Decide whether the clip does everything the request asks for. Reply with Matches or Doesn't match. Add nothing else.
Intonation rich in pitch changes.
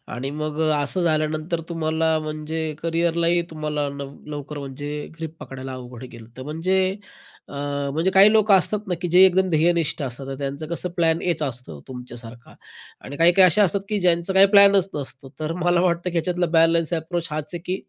Doesn't match